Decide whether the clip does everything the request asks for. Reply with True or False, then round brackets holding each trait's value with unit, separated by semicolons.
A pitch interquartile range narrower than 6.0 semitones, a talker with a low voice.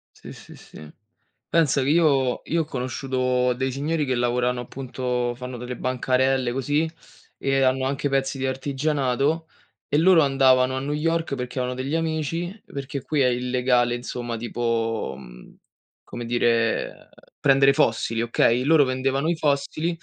True (2.5 semitones; 130 Hz)